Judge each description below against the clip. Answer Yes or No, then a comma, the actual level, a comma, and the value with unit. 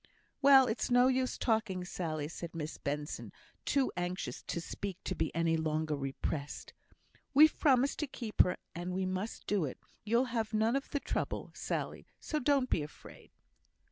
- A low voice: No, high, 190 Hz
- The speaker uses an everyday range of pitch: No, wide, 7.6 semitones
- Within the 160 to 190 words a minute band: Yes, average, 170 wpm